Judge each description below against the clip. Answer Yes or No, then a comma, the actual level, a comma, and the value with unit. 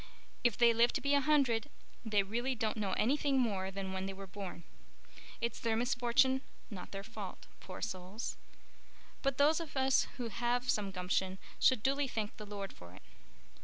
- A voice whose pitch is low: No, high, 225 Hz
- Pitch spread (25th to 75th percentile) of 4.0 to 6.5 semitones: Yes, average, 4.8 semitones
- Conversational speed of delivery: Yes, average, 180 wpm